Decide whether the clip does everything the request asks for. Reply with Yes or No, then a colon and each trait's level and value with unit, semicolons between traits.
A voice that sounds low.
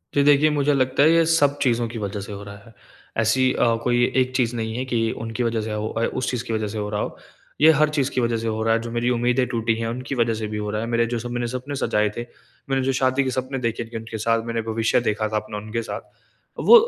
Yes: low, 115 Hz